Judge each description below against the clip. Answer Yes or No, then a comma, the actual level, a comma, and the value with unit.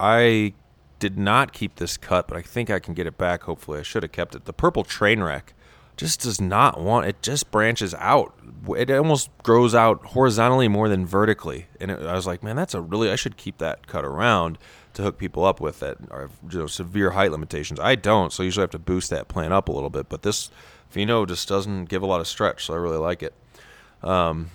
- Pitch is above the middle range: No, very low, 95 Hz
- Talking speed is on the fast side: Yes, fast, 240 wpm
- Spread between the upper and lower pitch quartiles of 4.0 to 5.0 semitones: Yes, average, 4.6 semitones